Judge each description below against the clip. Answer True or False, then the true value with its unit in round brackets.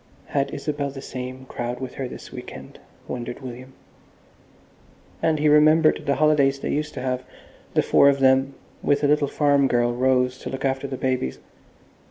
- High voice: False (135 Hz)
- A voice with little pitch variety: True (1.9 semitones)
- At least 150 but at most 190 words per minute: True (180 wpm)